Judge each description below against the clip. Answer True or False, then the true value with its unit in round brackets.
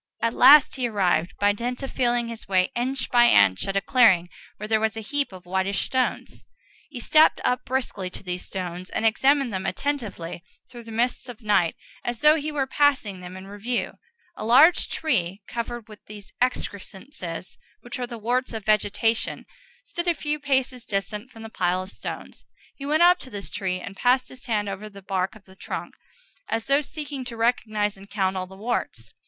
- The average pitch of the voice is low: False (225 Hz)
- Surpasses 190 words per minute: True (200 wpm)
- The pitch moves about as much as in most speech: True (4.8 semitones)